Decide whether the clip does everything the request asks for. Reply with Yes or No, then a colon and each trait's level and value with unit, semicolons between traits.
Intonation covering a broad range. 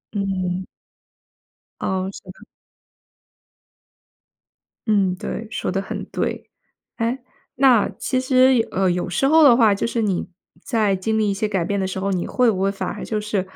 No: average, 3.5 semitones